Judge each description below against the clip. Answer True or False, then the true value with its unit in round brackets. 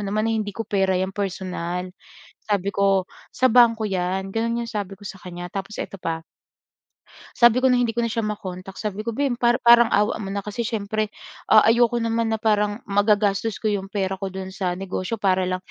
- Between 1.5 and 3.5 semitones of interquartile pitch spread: True (2.8 semitones)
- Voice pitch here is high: True (205 Hz)